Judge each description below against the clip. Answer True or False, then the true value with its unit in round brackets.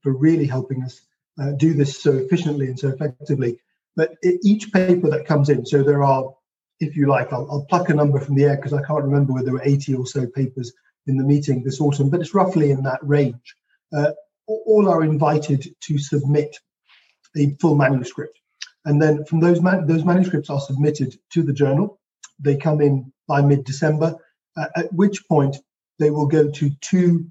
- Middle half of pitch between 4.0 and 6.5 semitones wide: False (2.7 semitones)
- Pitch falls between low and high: True (145 Hz)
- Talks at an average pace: True (195 wpm)